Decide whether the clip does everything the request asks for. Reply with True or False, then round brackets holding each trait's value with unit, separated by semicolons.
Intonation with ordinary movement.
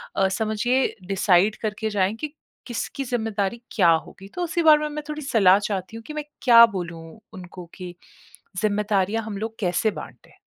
True (3.7 semitones)